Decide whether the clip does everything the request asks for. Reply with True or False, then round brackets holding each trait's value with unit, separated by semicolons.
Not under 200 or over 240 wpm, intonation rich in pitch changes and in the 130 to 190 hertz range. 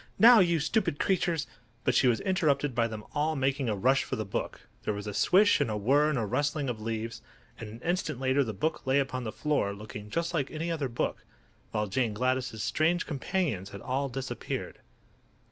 True (205 wpm; 5.8 semitones; 135 Hz)